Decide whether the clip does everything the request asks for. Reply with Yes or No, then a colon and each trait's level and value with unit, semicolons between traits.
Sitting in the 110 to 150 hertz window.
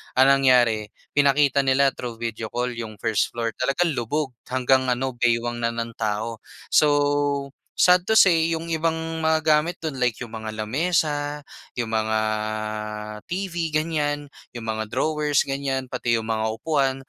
Yes: low, 135 Hz